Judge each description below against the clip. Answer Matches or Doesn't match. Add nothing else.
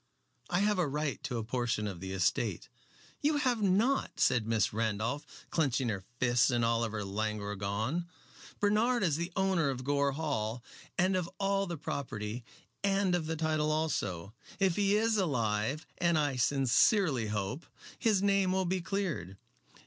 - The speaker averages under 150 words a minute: Doesn't match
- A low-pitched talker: Doesn't match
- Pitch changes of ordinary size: Doesn't match